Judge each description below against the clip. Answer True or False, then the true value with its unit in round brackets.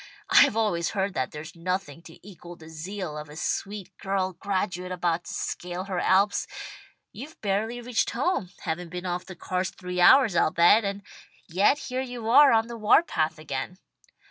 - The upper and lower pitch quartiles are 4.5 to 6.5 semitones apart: False (3.6 semitones)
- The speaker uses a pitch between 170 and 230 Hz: True (185 Hz)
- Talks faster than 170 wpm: True (180 wpm)